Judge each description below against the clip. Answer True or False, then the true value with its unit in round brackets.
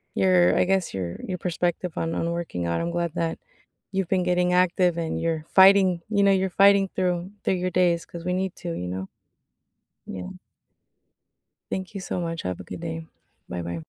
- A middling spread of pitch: False (2.3 semitones)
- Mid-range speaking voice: True (175 Hz)